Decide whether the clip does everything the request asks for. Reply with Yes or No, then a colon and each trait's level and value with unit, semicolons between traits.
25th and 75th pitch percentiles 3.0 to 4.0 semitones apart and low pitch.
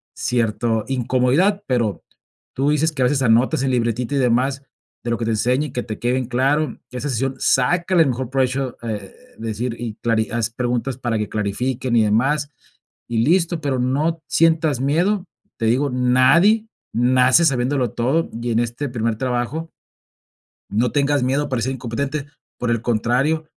Yes: average, 3.3 semitones; low, 125 Hz